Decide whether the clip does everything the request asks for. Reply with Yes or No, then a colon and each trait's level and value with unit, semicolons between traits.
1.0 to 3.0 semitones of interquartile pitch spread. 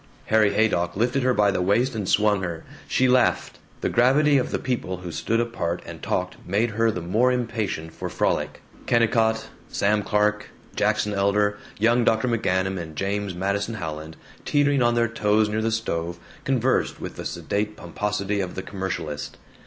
No: average, 3.5 semitones